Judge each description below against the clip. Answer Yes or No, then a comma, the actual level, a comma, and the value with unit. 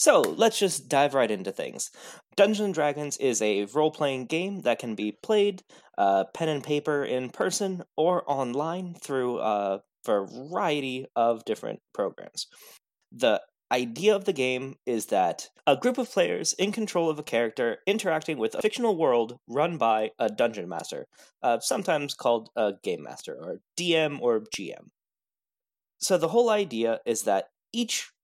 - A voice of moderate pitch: Yes, medium, 155 Hz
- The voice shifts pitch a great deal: Yes, wide, 8.3 semitones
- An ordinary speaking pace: Yes, average, 160 wpm